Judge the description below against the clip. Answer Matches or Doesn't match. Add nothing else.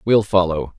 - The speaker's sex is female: Doesn't match